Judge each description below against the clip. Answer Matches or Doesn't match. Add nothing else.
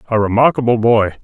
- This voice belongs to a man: Matches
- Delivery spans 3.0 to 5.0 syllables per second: Doesn't match